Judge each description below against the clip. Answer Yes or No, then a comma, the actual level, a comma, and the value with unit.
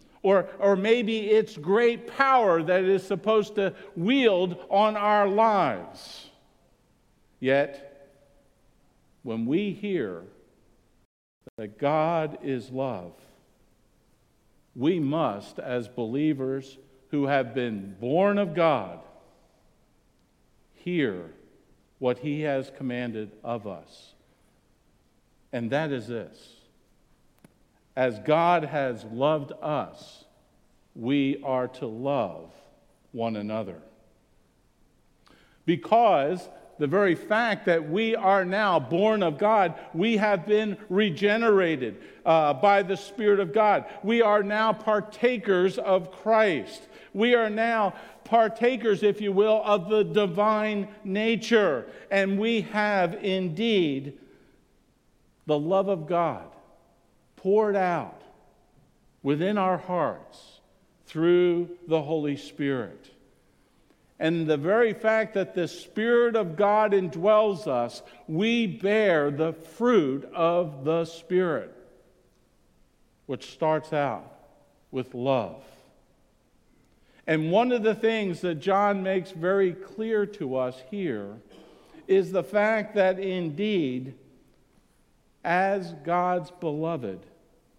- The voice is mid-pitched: Yes, medium, 180 Hz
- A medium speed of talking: No, slow, 105 wpm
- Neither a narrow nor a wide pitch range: No, wide, 6.7 semitones